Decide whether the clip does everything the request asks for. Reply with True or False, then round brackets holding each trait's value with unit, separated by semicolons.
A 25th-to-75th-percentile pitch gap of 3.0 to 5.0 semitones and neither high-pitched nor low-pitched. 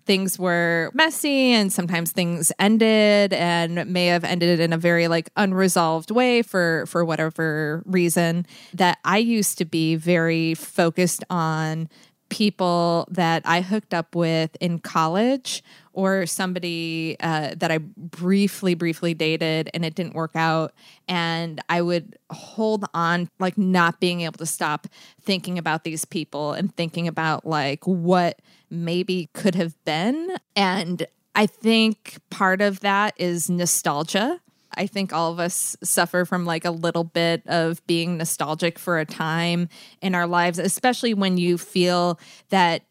False (2.5 semitones; 175 Hz)